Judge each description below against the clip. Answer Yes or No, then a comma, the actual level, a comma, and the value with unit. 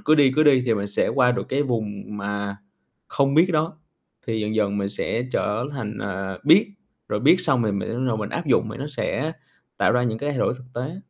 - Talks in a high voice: No, low, 125 Hz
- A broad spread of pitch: Yes, wide, 5.7 semitones